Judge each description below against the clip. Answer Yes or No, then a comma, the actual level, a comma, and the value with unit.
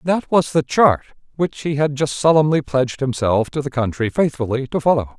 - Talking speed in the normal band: Yes, average, 195 wpm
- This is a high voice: No, medium, 140 Hz